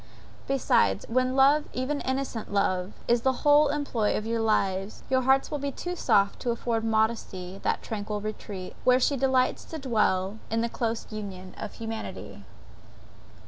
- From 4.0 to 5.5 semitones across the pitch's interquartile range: Yes, average, 4.3 semitones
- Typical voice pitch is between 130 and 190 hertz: No, high, 230 Hz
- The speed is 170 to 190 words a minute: No, average, 155 wpm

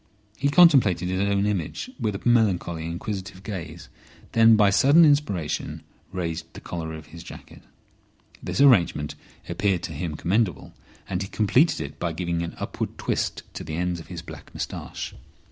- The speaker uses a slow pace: No, average, 165 wpm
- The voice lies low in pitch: Yes, very low, 90 Hz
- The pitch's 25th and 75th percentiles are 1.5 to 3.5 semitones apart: No, average, 4.6 semitones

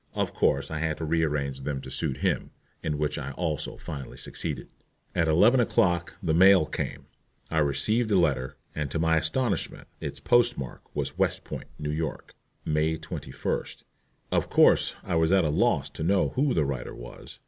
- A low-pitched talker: Yes, very low, 80 Hz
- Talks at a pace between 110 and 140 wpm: No, average, 180 wpm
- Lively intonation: No, average, 3.7 semitones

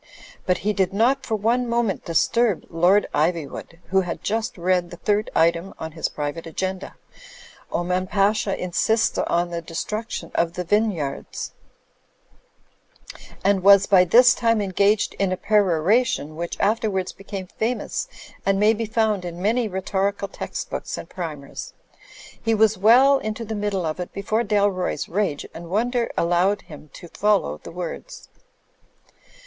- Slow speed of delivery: No, average, 155 wpm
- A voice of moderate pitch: No, high, 195 Hz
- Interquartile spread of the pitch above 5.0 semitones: No, average, 3.8 semitones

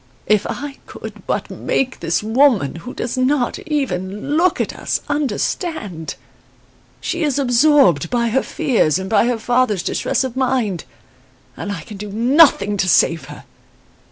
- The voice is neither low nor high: No, high, 240 Hz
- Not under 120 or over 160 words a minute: Yes, average, 155 wpm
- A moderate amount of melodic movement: No, wide, 5.7 semitones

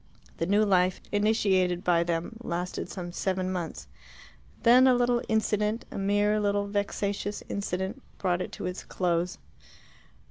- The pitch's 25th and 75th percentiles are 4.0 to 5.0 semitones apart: No, average, 2.7 semitones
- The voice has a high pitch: Yes, high, 200 Hz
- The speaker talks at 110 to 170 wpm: Yes, average, 140 wpm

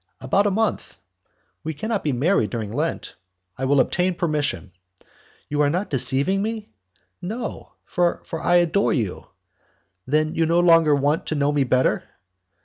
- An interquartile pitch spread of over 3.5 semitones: Yes, average, 4.1 semitones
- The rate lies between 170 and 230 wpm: No, average, 150 wpm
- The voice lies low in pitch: No, medium, 155 Hz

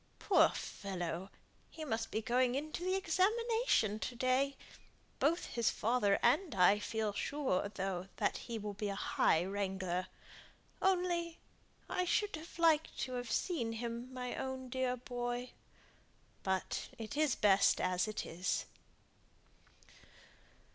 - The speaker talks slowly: Yes, slow, 130 wpm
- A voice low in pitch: No, high, 240 Hz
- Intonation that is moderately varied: No, wide, 6.6 semitones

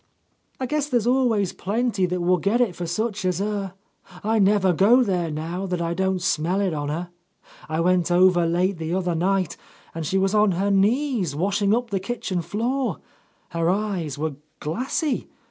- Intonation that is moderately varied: Yes, average, 3.6 semitones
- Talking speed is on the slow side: No, average, 180 wpm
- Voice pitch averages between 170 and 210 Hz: Yes, high, 190 Hz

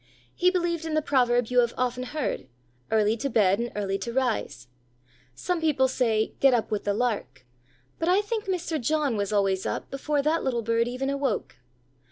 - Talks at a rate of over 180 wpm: Yes, average, 190 wpm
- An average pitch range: No, wide, 5.7 semitones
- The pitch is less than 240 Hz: No, very high, 250 Hz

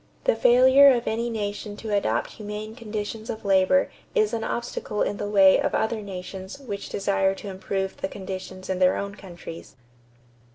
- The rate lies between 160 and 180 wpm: Yes, average, 170 wpm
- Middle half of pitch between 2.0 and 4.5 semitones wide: Yes, average, 2.8 semitones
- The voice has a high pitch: Yes, high, 205 Hz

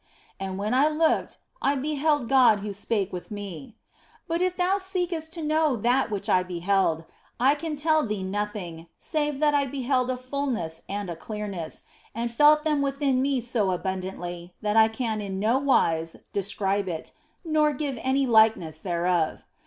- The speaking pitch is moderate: No, high, 230 Hz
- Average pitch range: No, wide, 6.9 semitones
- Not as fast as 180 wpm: Yes, average, 170 wpm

